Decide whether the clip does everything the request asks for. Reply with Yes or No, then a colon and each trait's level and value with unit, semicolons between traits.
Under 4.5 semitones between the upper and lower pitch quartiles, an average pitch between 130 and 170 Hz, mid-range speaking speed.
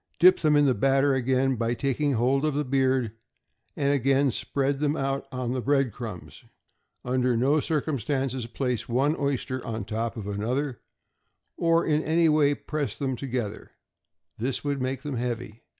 Yes: average, 2.7 semitones; low, 135 Hz; average, 165 wpm